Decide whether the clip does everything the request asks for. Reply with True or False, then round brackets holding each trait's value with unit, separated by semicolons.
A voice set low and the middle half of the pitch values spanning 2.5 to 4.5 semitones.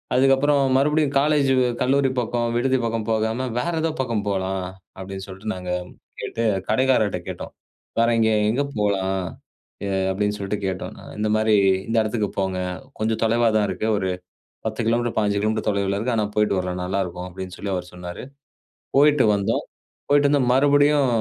False (110 Hz; 5.1 semitones)